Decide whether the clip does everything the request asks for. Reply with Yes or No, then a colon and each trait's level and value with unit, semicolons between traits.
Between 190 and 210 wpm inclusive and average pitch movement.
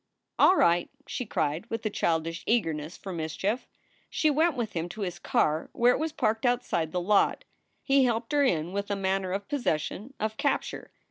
No: average, 195 wpm; wide, 6.3 semitones